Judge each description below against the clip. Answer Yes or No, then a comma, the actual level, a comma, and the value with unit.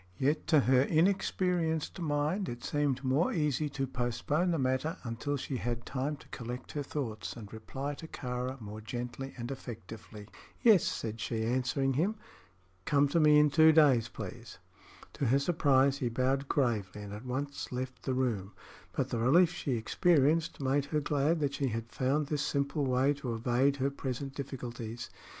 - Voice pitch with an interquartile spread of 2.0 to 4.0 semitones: Yes, average, 3.4 semitones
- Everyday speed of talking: Yes, average, 170 wpm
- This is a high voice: No, low, 135 Hz